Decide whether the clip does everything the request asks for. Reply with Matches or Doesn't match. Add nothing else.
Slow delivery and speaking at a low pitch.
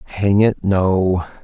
Matches